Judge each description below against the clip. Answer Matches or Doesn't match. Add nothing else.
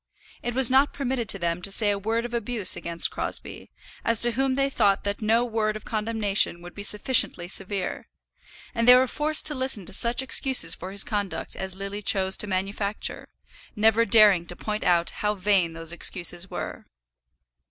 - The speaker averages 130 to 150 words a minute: Doesn't match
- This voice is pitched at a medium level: Doesn't match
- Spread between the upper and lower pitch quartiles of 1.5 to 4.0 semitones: Matches